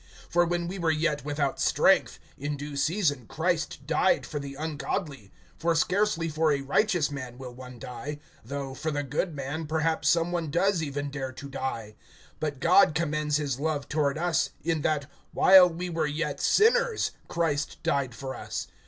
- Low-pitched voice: No, medium, 150 Hz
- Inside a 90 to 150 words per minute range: No, average, 175 wpm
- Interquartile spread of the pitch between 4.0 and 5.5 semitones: No, average, 3.2 semitones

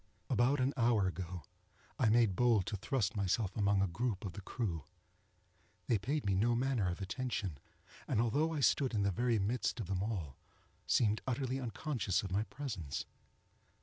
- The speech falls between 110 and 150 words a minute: No, average, 175 wpm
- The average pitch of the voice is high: No, low, 110 Hz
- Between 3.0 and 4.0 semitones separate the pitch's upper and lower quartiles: No, average, 4.5 semitones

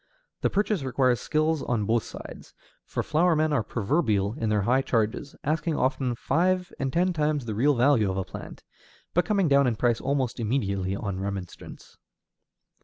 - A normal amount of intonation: No, wide, 6.0 semitones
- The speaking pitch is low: Yes, low, 130 Hz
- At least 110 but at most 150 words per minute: No, average, 175 wpm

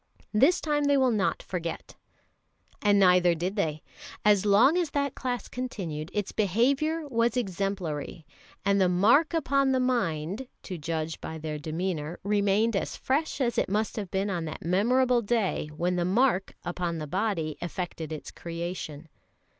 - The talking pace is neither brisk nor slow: Yes, average, 160 wpm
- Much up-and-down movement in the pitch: Yes, wide, 6.4 semitones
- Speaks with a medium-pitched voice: No, high, 195 Hz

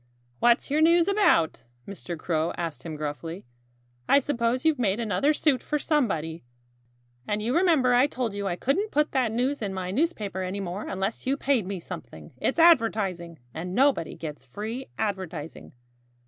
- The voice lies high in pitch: Yes, high, 220 Hz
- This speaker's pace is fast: No, average, 165 wpm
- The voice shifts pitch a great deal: Yes, wide, 7.5 semitones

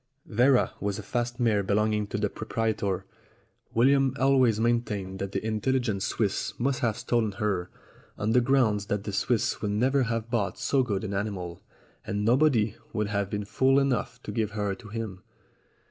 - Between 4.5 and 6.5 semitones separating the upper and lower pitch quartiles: No, average, 3.0 semitones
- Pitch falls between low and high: No, low, 110 Hz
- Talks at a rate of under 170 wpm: No, average, 175 wpm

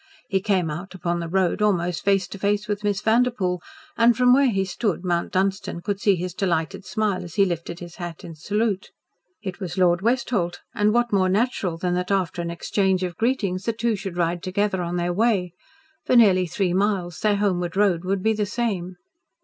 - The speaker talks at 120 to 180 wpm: No, fast, 205 wpm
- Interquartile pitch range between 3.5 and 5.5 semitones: No, average, 3.0 semitones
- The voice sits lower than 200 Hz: Yes, high, 190 Hz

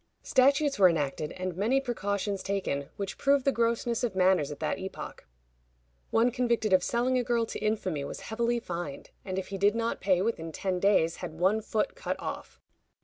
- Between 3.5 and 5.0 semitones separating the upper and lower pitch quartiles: Yes, average, 4.3 semitones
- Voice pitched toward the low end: No, high, 200 Hz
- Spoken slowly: No, average, 190 wpm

